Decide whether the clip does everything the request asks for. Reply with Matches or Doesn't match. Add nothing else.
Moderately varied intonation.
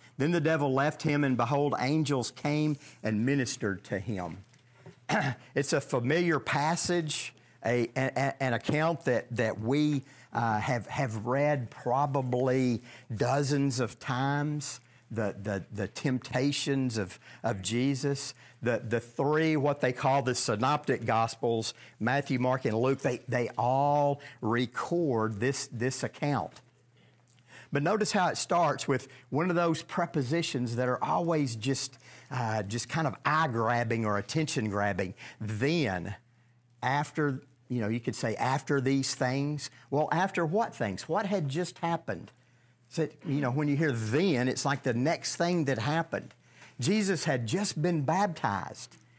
Matches